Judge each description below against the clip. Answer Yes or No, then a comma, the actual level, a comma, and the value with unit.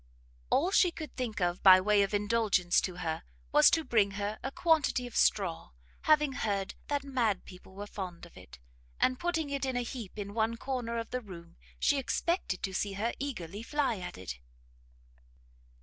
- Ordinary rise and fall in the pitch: No, wide, 6.0 semitones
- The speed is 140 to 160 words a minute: No, average, 185 wpm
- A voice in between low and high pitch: No, high, 220 Hz